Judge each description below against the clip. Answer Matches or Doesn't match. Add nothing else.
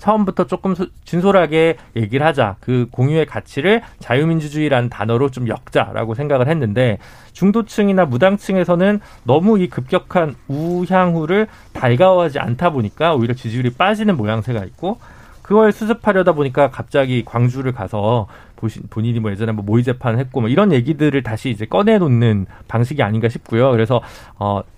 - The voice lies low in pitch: Matches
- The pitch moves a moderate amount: Doesn't match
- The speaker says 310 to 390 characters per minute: Matches